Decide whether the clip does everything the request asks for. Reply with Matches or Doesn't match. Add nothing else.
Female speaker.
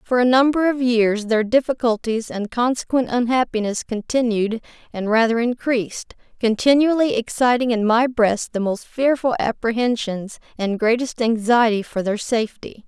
Matches